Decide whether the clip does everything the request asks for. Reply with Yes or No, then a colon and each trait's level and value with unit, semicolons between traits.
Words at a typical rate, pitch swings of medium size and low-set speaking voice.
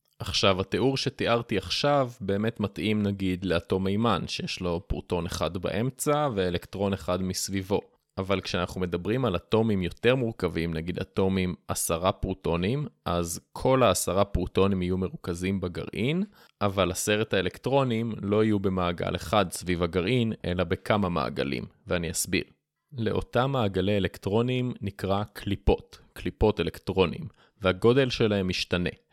Yes: average, 120 wpm; average, 3.8 semitones; low, 100 Hz